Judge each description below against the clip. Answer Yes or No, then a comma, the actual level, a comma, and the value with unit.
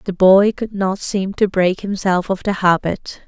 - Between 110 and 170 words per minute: No, average, 200 wpm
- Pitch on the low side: No, high, 190 Hz